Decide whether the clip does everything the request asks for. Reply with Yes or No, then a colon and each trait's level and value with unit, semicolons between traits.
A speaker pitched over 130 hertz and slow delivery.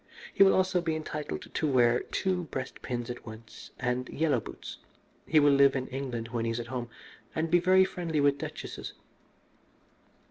No: medium, 140 Hz; average, 180 wpm